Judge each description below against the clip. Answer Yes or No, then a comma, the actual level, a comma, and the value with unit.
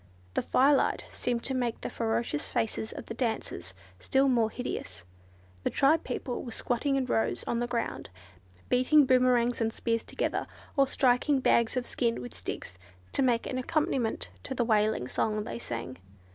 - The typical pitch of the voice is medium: No, high, 240 Hz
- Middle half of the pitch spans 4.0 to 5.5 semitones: No, narrow, 2.6 semitones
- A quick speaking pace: No, average, 170 wpm